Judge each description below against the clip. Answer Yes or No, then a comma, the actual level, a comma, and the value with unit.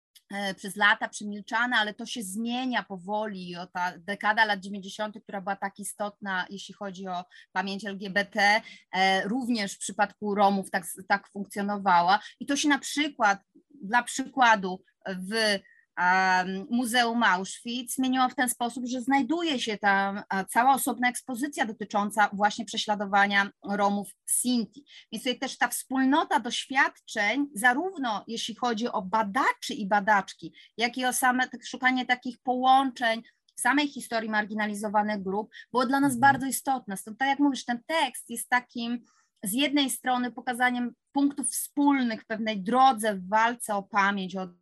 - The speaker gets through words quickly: No, average, 145 wpm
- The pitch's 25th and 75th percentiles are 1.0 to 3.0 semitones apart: No, average, 4.0 semitones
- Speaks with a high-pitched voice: Yes, high, 225 Hz